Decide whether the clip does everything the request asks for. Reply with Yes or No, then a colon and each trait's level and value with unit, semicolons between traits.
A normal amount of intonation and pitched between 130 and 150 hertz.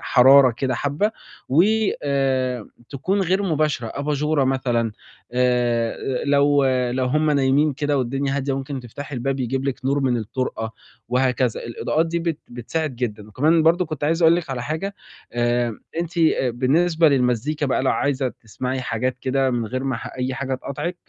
Yes: average, 3.3 semitones; low, 135 Hz